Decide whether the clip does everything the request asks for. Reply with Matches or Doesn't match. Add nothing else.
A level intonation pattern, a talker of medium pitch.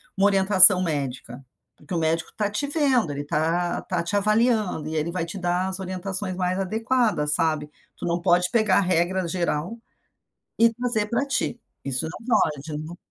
Doesn't match